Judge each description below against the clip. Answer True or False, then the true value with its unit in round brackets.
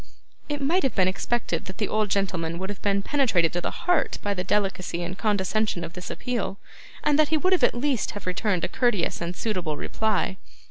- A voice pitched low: False (200 Hz)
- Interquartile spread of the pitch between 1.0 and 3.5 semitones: False (4.8 semitones)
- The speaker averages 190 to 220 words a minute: True (205 wpm)